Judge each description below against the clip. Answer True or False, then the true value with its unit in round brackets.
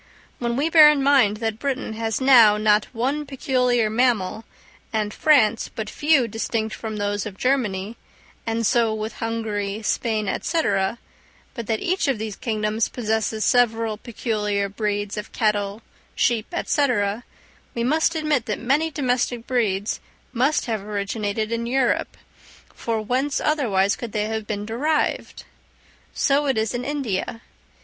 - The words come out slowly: False (145 wpm)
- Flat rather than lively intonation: False (3.4 semitones)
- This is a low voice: False (225 Hz)